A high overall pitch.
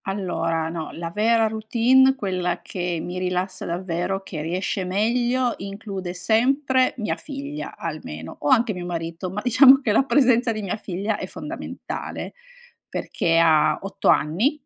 Yes: high, 195 Hz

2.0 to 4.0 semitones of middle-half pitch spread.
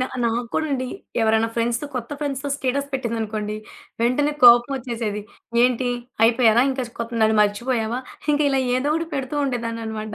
Yes: average, 2.8 semitones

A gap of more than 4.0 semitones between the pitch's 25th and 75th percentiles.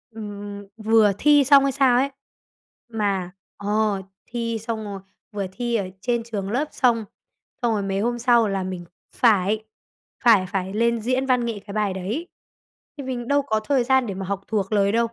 No: average, 3.3 semitones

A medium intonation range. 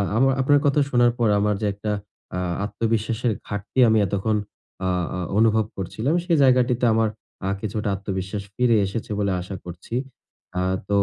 Yes: average, 3.2 semitones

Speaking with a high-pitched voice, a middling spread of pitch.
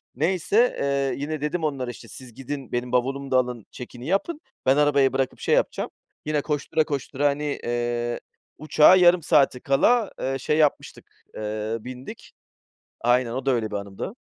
No: low, 135 Hz; average, 3.5 semitones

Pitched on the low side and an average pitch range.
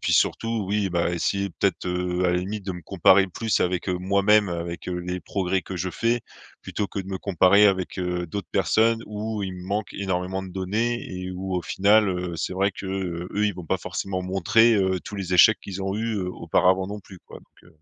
No: very low, 95 Hz; narrow, 2.0 semitones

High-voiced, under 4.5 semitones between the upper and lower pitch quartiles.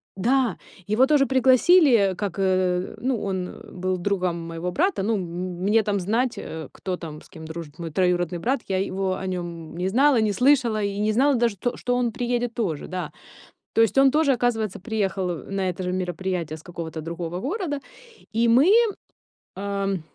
No: high, 195 Hz; average, 5.3 semitones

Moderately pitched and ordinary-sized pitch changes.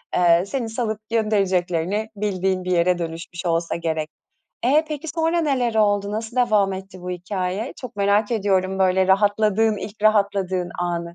No: high, 200 Hz; average, 3.2 semitones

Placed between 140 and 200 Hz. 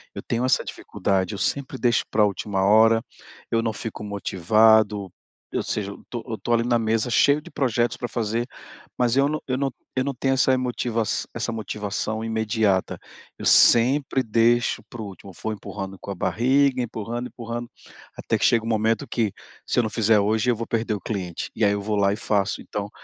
No: low, 115 Hz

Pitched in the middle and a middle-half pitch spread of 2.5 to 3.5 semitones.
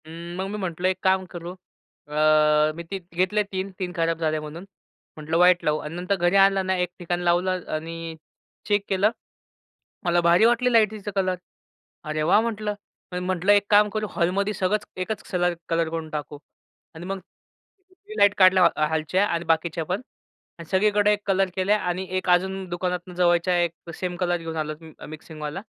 Yes: medium, 180 Hz; average, 2.8 semitones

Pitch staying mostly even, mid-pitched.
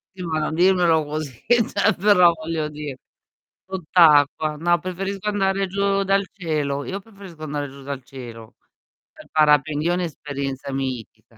No: average, 4.8 semitones; medium, 160 Hz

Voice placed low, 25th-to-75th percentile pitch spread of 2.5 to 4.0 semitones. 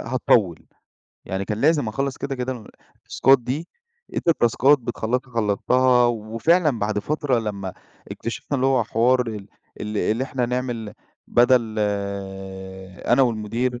Yes: low, 120 Hz; average, 3.1 semitones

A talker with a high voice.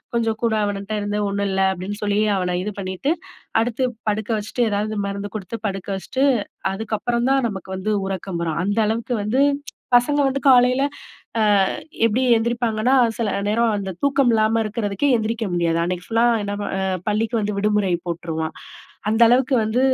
Yes: high, 215 Hz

